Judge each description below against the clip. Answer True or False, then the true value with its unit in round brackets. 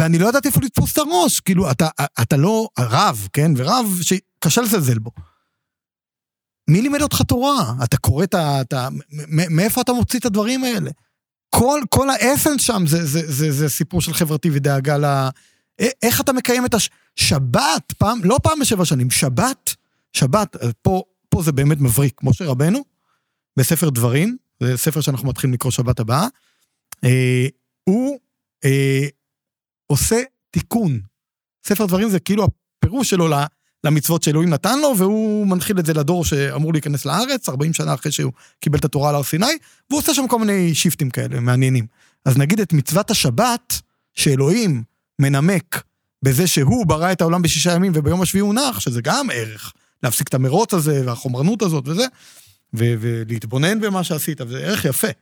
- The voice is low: False (155 Hz)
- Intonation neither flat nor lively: False (7.0 semitones)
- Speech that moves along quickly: True (165 wpm)